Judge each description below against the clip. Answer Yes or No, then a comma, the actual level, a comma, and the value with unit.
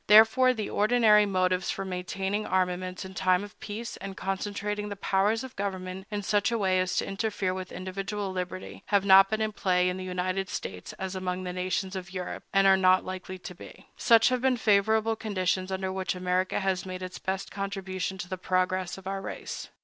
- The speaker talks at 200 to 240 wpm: Yes, fast, 205 wpm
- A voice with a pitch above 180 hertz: Yes, high, 190 Hz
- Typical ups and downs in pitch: No, narrow, 1.9 semitones